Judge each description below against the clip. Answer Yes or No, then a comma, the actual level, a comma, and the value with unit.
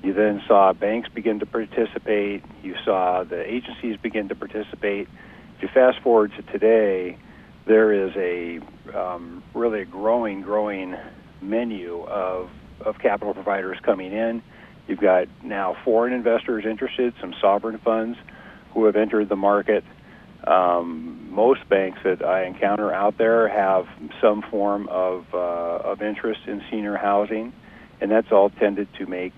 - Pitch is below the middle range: Yes, low, 100 Hz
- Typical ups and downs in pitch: Yes, average, 3.0 semitones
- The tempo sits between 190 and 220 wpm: No, average, 150 wpm